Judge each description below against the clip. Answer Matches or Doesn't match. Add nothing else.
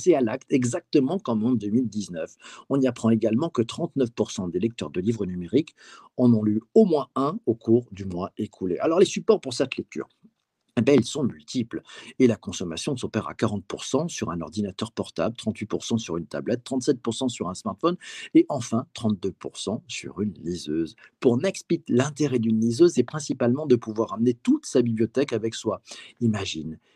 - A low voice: Matches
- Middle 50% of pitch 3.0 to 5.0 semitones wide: Matches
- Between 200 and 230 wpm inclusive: Doesn't match